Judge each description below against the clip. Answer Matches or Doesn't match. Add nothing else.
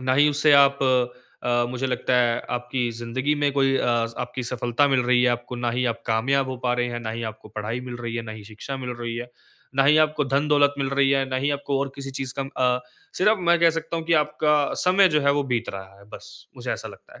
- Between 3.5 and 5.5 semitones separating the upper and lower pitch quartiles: Doesn't match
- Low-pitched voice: Matches